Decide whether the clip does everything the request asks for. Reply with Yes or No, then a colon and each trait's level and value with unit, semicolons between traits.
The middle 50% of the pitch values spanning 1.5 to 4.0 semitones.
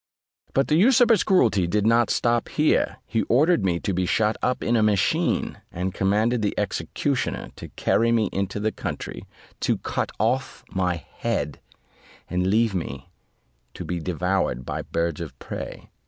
No: average, 4.6 semitones